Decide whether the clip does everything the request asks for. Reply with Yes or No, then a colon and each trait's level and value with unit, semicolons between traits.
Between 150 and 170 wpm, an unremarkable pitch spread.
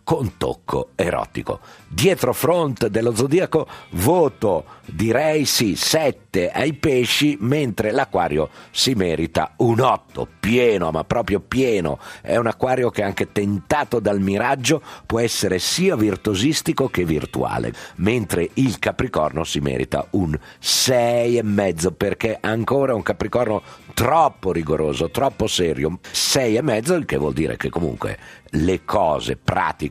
No: average, 135 wpm; average, 4.9 semitones